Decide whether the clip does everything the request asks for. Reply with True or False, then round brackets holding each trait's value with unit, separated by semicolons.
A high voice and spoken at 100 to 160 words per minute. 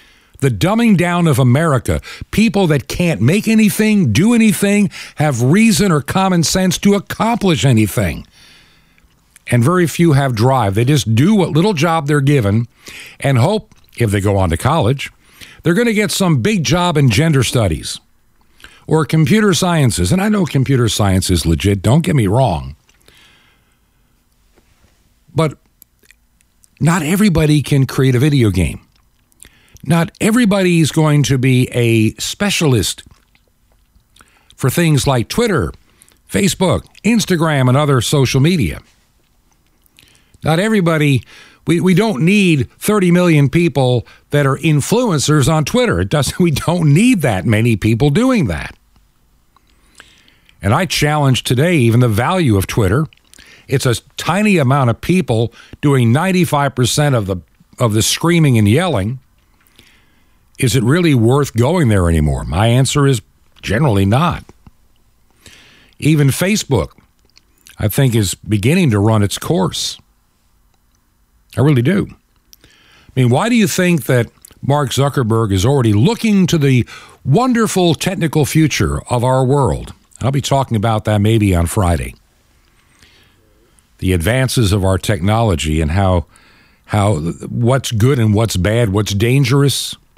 False (135 Hz; 140 wpm)